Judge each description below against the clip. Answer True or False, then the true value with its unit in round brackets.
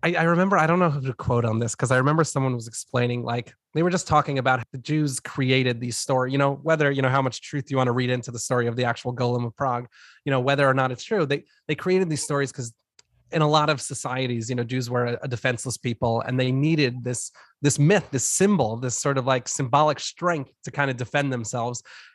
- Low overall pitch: True (130 Hz)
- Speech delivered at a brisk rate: True (250 wpm)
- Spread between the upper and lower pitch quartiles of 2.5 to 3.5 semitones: True (2.9 semitones)